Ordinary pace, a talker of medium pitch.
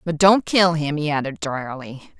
Yes: average, 190 wpm; medium, 160 Hz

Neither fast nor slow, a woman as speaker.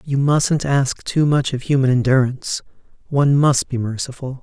No: average, 165 wpm; male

